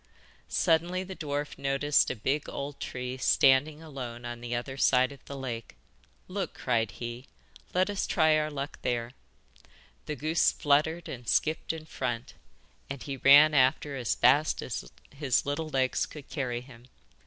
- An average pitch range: Yes, average, 3.5 semitones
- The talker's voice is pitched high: No, medium, 140 Hz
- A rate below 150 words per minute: No, average, 160 wpm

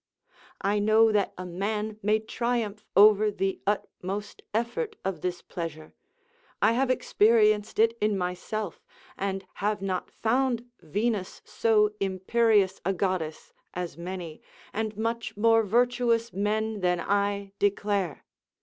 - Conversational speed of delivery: No, slow, 125 wpm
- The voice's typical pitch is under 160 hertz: No, high, 210 Hz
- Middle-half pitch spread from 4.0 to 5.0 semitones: No, average, 2.7 semitones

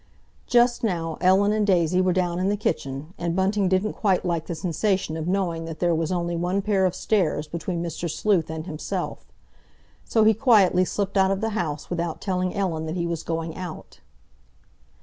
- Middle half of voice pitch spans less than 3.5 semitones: Yes, average, 3.0 semitones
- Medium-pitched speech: Yes, medium, 180 Hz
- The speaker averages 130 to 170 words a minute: No, average, 190 wpm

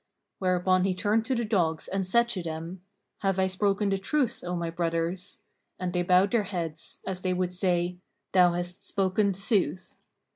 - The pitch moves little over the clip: Yes, narrow, 1.9 semitones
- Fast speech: No, average, 180 wpm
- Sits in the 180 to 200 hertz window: Yes, medium, 185 Hz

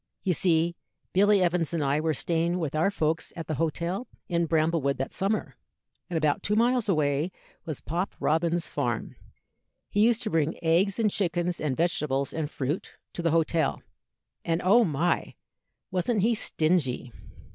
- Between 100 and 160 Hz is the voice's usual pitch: No, medium, 170 Hz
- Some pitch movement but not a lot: Yes, average, 3.2 semitones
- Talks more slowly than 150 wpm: No, average, 160 wpm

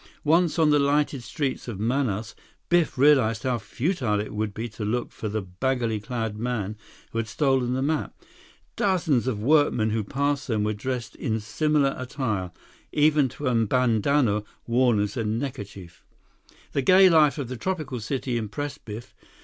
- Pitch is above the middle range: No, low, 125 Hz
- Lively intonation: No, average, 4.7 semitones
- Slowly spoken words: No, average, 165 wpm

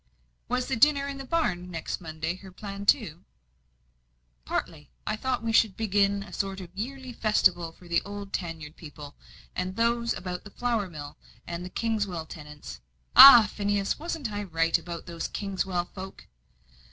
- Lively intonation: No, average, 4.7 semitones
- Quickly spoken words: No, average, 165 wpm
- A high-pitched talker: Yes, high, 195 Hz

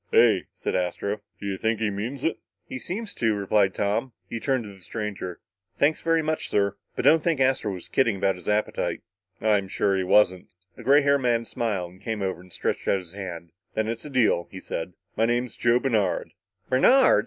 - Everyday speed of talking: No, fast, 210 wpm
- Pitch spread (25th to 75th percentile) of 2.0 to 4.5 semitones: No, average, 5.0 semitones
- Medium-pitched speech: No, low, 110 Hz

